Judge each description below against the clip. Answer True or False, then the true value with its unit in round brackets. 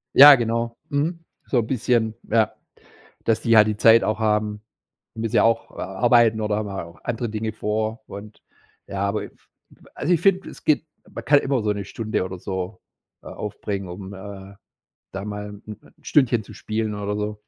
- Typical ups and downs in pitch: False (2.2 semitones)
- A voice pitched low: True (110 Hz)